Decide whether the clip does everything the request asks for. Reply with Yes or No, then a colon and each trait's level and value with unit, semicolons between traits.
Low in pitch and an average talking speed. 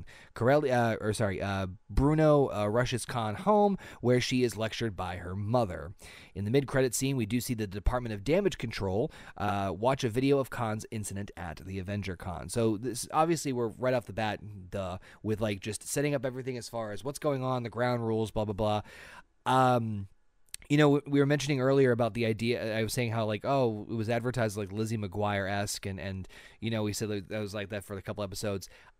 No: low, 110 Hz; fast, 215 wpm